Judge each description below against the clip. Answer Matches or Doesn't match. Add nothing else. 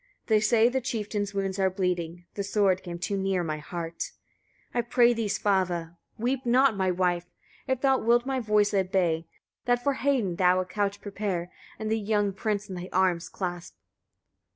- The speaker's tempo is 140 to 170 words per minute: Doesn't match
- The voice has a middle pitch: Doesn't match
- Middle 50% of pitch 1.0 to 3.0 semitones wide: Doesn't match